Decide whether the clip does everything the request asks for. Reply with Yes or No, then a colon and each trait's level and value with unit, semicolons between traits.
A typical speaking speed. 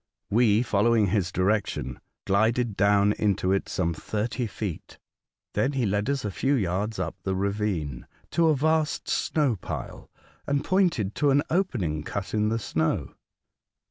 Yes: average, 155 wpm